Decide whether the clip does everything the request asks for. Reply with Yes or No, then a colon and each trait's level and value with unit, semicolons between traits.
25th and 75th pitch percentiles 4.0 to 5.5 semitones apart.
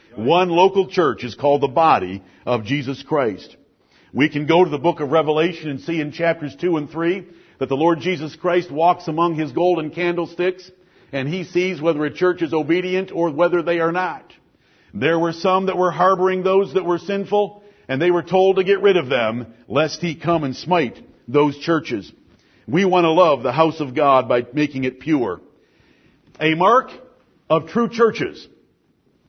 No: average, 3.4 semitones